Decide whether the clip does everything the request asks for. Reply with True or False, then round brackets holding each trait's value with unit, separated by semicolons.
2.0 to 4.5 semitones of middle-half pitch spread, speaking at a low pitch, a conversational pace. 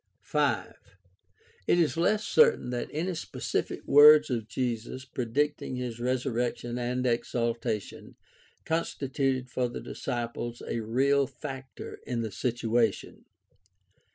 False (3.0 semitones; 125 Hz; 115 wpm)